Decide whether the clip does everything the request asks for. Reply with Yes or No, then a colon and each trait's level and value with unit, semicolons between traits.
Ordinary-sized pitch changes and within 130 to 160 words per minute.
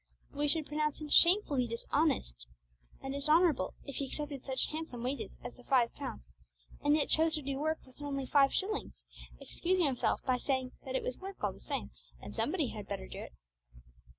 No: average, 3.3 semitones; average, 195 wpm